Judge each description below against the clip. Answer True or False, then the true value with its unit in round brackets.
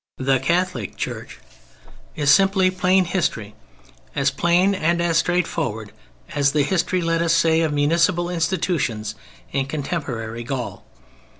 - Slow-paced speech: True (125 wpm)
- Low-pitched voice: False (165 Hz)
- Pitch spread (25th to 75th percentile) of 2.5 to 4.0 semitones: False (4.6 semitones)